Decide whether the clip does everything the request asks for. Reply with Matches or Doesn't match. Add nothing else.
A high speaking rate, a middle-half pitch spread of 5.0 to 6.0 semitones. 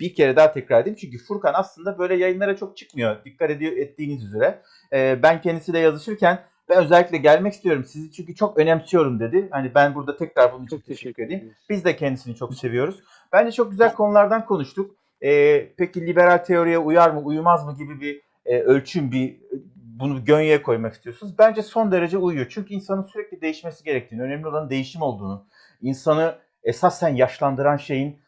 Matches